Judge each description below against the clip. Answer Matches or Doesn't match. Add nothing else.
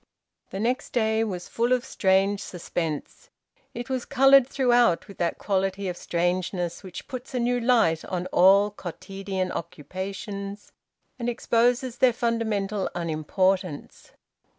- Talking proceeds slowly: Matches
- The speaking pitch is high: Matches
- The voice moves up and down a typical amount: Matches